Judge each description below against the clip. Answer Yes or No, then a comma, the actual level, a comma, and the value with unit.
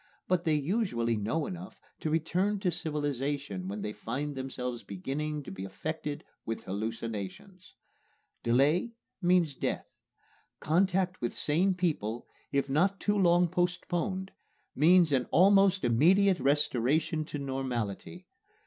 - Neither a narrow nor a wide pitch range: No, wide, 6.3 semitones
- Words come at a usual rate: No, slow, 120 wpm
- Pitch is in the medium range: Yes, medium, 150 Hz